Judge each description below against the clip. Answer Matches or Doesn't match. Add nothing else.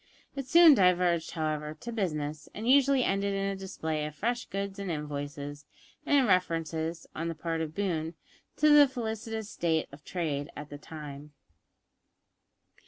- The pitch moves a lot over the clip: Matches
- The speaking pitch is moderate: Matches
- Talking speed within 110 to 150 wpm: Doesn't match